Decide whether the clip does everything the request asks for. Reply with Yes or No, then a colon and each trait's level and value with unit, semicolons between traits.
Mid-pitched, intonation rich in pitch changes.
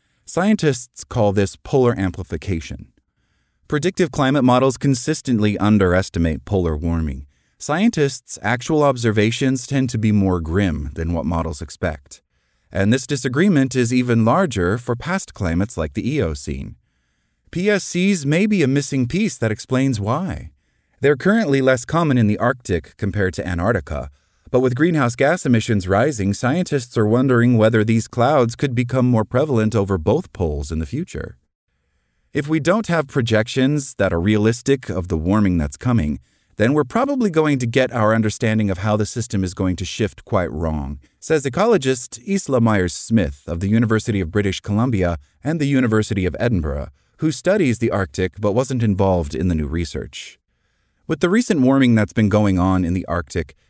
No: low, 110 Hz; wide, 6.6 semitones